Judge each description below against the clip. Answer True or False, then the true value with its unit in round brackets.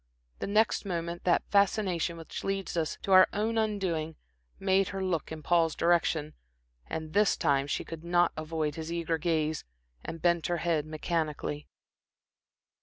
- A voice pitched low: False (170 Hz)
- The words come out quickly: False (155 wpm)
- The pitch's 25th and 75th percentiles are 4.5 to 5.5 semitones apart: False (3.1 semitones)